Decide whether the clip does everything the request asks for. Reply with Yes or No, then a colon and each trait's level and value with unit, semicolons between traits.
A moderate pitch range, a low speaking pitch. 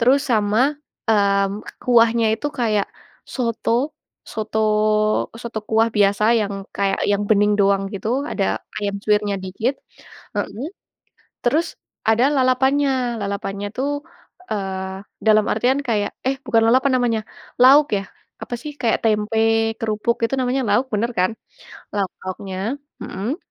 No: average, 3.6 semitones; high, 225 Hz